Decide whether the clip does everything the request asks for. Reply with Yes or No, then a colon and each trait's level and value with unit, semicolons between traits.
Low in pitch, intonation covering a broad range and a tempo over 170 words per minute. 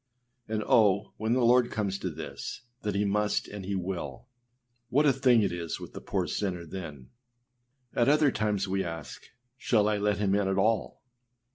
No: low, 100 Hz; average, 2.8 semitones; average, 190 wpm